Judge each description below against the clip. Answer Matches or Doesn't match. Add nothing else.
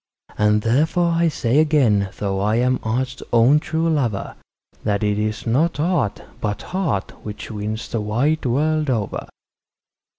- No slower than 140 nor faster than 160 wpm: Matches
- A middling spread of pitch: Doesn't match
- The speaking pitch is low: Matches